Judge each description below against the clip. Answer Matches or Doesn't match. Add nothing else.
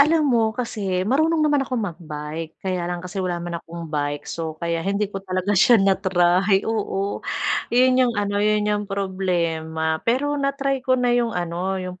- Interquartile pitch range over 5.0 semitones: Matches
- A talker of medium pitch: Doesn't match